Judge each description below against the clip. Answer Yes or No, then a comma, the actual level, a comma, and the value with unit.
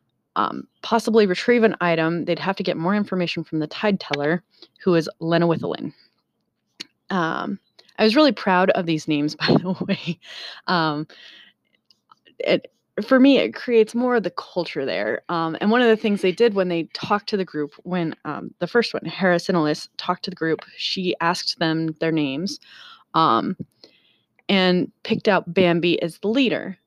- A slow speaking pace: No, average, 175 wpm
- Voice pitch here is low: No, medium, 180 Hz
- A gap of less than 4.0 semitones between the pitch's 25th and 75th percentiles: No, average, 4.3 semitones